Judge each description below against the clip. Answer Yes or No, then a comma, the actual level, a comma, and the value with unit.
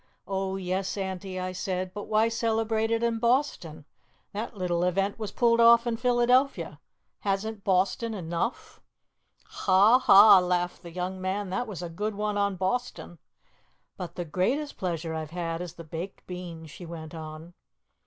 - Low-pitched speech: No, high, 190 Hz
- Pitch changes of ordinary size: Yes, average, 4.0 semitones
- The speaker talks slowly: No, average, 160 wpm